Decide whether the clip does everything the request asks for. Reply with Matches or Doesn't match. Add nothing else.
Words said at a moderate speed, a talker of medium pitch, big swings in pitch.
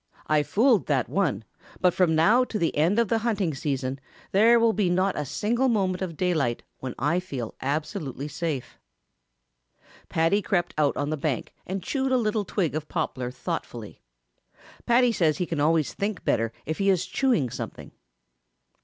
Matches